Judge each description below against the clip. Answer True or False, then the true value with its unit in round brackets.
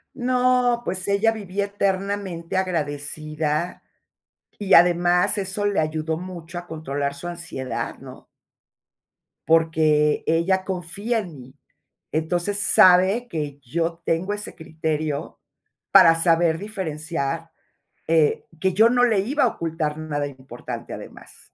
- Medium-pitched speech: True (170 Hz)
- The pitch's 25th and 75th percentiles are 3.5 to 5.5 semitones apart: True (4.1 semitones)